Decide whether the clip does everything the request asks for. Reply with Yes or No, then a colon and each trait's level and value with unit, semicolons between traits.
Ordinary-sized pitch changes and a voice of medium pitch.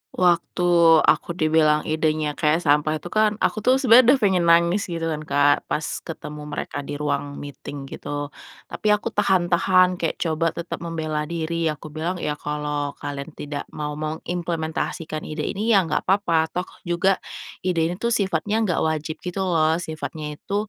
Yes: average, 3.1 semitones; medium, 165 Hz